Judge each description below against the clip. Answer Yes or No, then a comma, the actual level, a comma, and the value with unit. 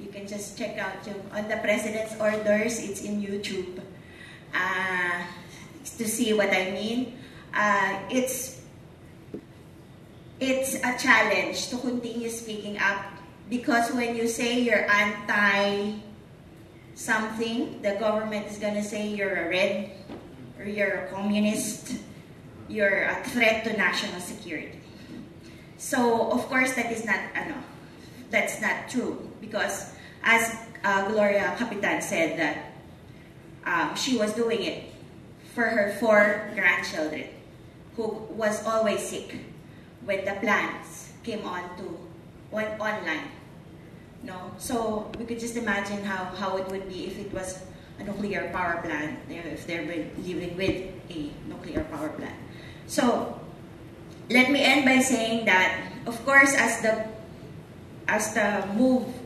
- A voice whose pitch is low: No, high, 210 Hz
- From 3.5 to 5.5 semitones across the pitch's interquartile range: No, average, 3.0 semitones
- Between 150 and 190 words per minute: No, slow, 135 wpm